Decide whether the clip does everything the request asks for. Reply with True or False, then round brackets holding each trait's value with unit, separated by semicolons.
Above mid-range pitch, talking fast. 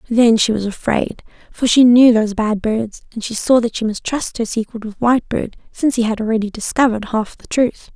True (225 Hz; 220 wpm)